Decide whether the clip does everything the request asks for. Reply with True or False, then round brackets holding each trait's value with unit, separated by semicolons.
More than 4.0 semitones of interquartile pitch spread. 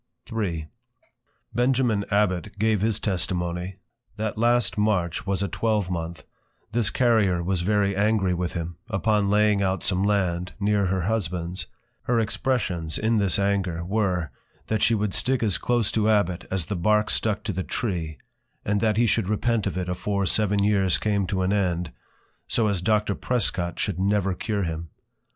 False (3.0 semitones)